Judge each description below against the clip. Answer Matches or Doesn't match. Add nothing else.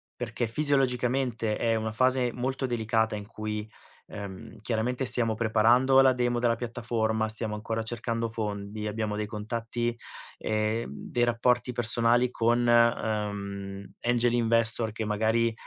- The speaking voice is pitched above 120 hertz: Doesn't match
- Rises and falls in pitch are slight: Matches